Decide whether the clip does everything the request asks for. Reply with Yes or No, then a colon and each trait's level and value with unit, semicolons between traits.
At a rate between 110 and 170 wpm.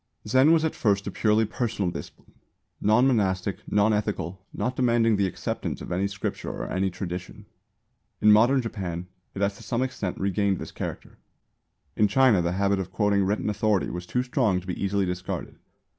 No: average, 180 wpm